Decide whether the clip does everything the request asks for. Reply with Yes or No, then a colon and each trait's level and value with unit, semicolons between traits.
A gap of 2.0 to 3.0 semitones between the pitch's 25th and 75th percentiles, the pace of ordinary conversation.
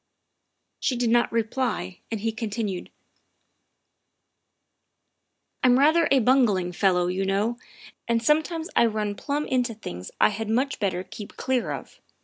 No: average, 4.3 semitones; average, 150 wpm